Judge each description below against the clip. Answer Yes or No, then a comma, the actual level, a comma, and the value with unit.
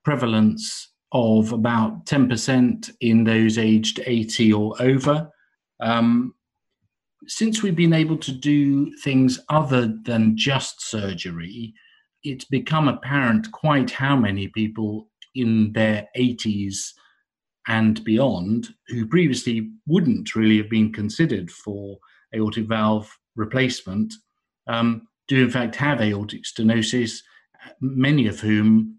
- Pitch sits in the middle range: No, low, 115 Hz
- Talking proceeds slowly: Yes, slow, 115 wpm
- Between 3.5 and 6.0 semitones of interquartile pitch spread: Yes, average, 4.2 semitones